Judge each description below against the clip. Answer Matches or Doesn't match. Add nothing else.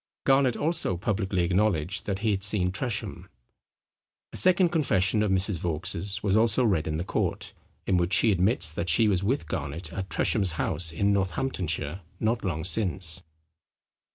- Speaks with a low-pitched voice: Matches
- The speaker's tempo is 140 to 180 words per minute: Matches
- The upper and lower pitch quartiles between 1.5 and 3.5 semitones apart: Doesn't match